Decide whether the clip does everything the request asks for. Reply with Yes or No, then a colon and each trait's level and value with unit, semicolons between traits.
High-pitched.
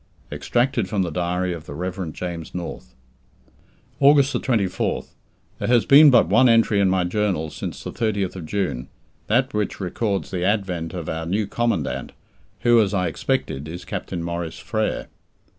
No: very low, 95 Hz